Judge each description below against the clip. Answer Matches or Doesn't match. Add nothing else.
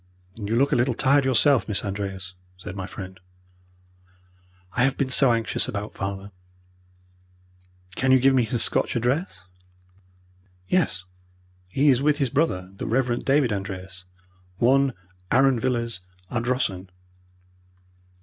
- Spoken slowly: Matches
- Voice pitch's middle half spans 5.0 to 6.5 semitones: Matches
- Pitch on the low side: Matches